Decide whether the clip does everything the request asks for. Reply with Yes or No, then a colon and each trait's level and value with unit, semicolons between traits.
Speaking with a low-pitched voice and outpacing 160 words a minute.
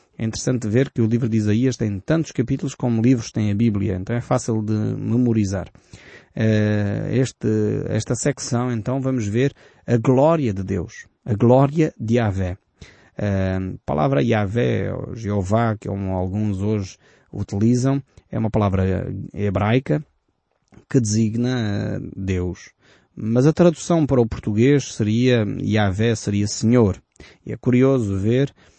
No: low, 115 Hz; average, 135 wpm